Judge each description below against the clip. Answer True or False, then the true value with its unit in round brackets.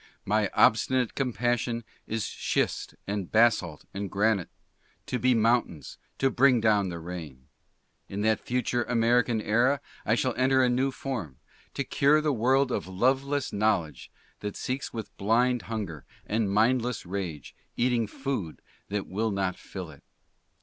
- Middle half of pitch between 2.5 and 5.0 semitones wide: True (4.2 semitones)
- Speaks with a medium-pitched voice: False (115 Hz)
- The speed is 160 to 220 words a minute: False (145 wpm)